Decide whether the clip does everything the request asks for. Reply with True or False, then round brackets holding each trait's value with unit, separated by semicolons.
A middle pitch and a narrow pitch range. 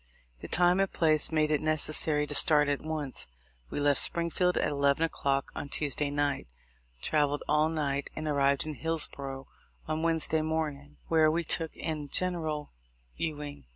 True (150 Hz; 1.9 semitones)